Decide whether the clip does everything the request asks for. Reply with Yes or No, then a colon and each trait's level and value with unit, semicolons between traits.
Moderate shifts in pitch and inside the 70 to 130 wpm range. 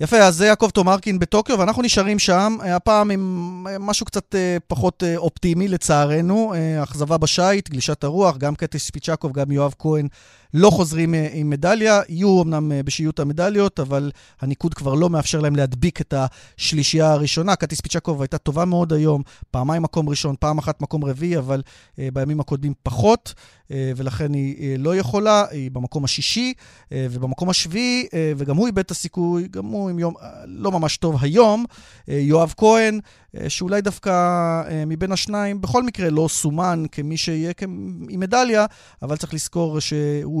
No: average, 4.4 semitones; fast, 150 wpm